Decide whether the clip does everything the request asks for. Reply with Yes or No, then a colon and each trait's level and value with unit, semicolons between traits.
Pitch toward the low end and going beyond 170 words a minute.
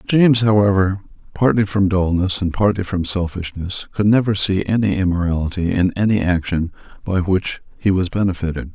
No: very low, 95 Hz; average, 150 wpm